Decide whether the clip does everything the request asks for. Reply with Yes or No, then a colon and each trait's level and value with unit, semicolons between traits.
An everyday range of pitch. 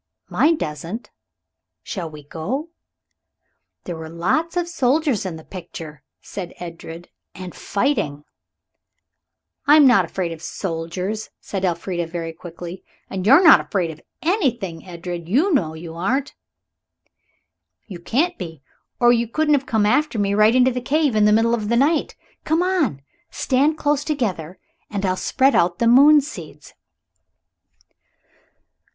No: wide, 8.3 semitones